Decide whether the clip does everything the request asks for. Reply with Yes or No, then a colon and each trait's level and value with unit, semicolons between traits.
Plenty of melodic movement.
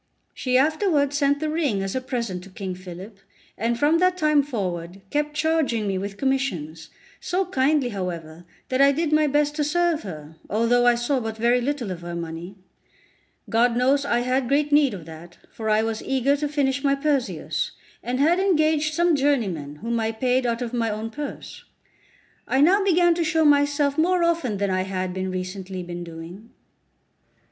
Yes: wide, 7.2 semitones